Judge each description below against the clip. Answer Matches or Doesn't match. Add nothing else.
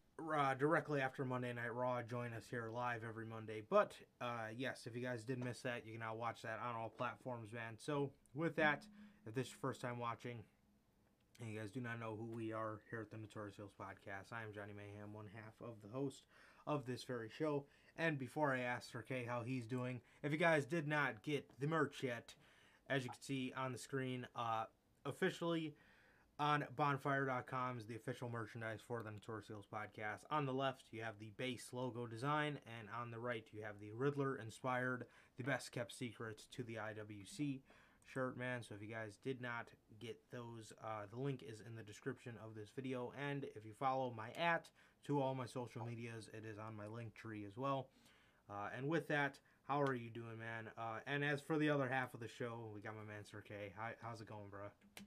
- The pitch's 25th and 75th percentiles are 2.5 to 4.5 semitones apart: Matches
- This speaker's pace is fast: Matches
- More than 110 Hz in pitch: Matches